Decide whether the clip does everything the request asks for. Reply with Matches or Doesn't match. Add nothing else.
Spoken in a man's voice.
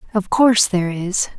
Doesn't match